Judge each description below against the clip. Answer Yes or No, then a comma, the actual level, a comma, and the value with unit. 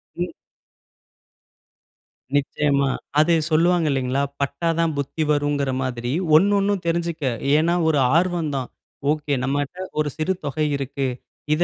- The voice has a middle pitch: Yes, medium, 150 Hz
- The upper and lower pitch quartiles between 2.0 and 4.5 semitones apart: Yes, average, 3.4 semitones